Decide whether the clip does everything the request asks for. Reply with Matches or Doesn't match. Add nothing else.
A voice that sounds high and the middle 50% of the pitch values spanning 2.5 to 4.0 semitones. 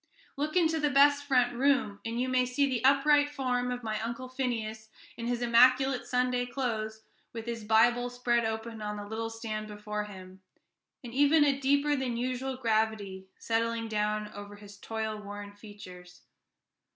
Matches